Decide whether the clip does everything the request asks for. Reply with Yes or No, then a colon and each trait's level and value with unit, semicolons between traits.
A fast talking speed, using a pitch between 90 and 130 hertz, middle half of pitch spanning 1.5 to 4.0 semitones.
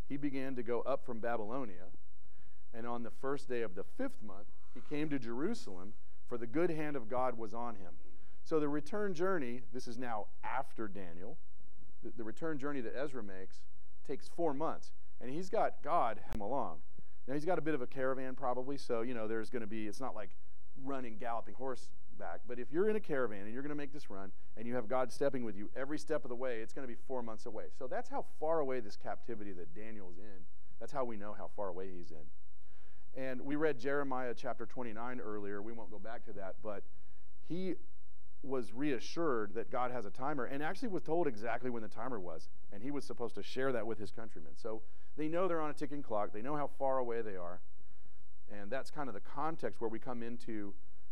No: fast, 225 wpm; low, 120 Hz; average, 4.8 semitones